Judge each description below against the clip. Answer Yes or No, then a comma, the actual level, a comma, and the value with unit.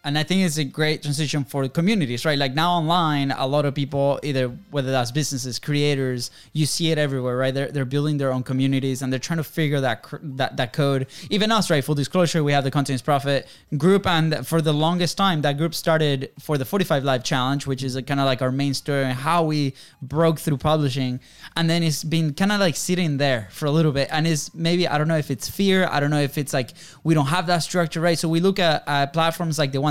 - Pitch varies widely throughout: No, average, 3.2 semitones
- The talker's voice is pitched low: No, medium, 150 Hz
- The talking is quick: Yes, fast, 245 wpm